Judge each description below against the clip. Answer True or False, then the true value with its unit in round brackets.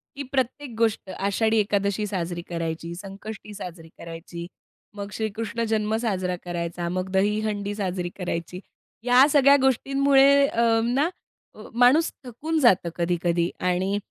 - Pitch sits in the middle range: False (205 Hz)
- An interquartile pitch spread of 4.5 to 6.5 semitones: True (5.1 semitones)